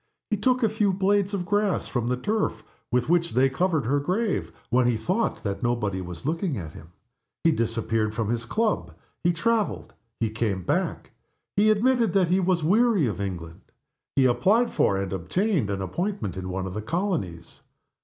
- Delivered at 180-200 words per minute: Yes, average, 185 wpm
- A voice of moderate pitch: Yes, medium, 145 Hz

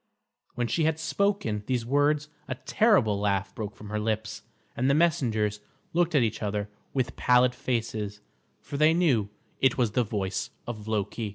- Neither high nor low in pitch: No, low, 120 Hz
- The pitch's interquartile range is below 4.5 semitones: No, average, 5.1 semitones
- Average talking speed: Yes, average, 170 wpm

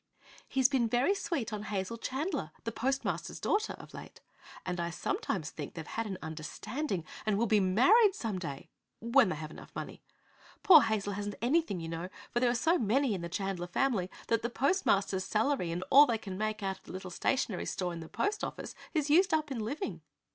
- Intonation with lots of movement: Yes, wide, 6.4 semitones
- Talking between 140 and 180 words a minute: No, fast, 205 wpm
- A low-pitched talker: No, high, 220 Hz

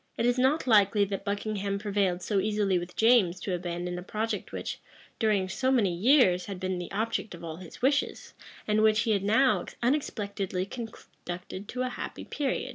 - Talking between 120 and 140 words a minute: No, average, 185 wpm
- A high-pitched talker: Yes, high, 205 Hz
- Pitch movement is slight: No, average, 3.7 semitones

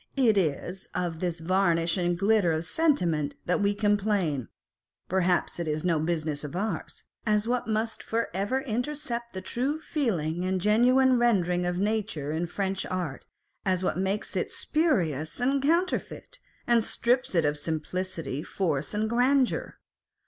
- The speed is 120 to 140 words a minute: No, average, 150 wpm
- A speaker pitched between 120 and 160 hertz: No, high, 190 Hz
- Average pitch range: No, wide, 5.8 semitones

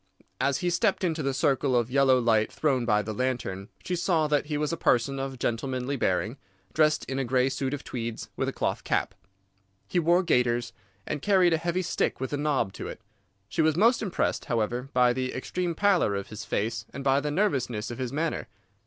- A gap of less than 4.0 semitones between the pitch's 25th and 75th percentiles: No, average, 4.6 semitones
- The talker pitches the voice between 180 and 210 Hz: No, low, 135 Hz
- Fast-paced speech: Yes, fast, 210 wpm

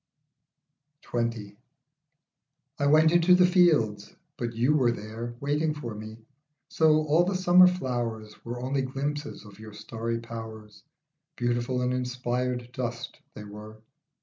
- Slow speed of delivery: Yes, slow, 130 wpm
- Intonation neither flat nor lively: Yes, average, 4.8 semitones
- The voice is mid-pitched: No, low, 125 Hz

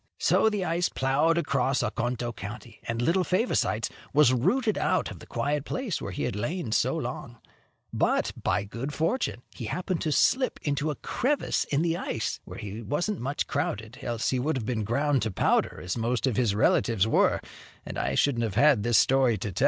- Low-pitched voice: Yes, low, 130 Hz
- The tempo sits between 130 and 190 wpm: No, average, 200 wpm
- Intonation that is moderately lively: No, wide, 6.1 semitones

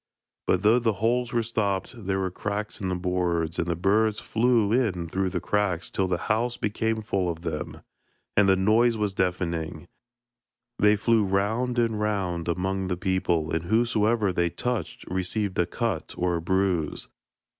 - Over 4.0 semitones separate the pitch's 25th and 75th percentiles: No, average, 3.6 semitones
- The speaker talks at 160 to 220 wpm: Yes, average, 170 wpm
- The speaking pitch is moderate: No, very low, 95 Hz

